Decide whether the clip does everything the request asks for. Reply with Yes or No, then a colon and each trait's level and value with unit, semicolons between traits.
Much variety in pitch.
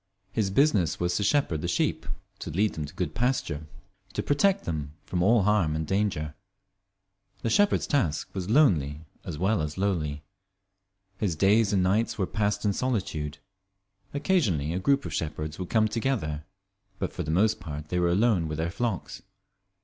Yes: wide, 6.0 semitones